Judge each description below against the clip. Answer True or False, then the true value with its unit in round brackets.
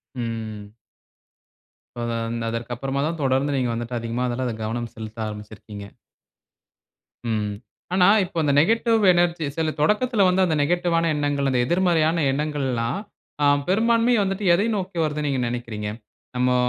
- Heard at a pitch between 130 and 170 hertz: True (140 Hz)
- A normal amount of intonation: False (6.9 semitones)